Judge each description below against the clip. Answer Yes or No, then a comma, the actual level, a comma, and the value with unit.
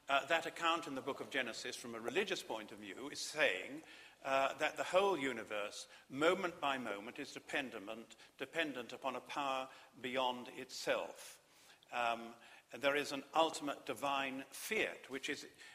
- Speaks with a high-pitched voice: No, low, 135 Hz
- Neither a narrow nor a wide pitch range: Yes, average, 3.3 semitones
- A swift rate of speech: No, average, 160 wpm